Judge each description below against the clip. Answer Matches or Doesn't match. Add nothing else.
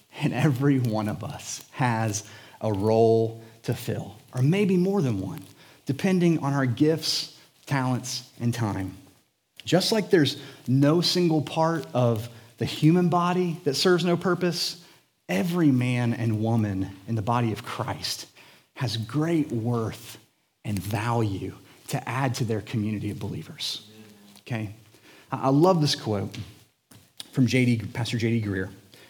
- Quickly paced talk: Doesn't match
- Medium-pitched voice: Doesn't match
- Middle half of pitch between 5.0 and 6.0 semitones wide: Matches